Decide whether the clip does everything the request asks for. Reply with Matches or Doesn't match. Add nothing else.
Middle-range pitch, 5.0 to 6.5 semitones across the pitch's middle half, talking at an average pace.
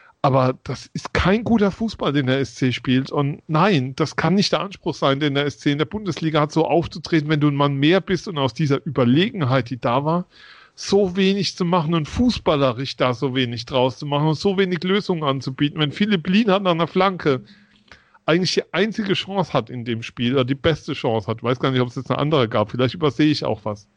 Doesn't match